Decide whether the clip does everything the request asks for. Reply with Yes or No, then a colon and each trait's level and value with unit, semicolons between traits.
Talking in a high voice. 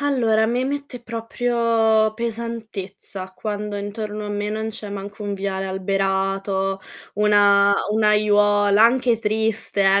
Yes: high, 210 Hz